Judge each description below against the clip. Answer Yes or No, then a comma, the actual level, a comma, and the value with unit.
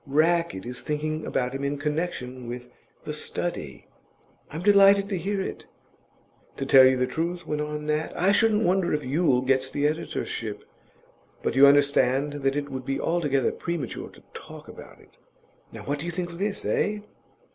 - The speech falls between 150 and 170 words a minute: No, average, 180 wpm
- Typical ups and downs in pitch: Yes, average, 4.4 semitones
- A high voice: No, medium, 150 Hz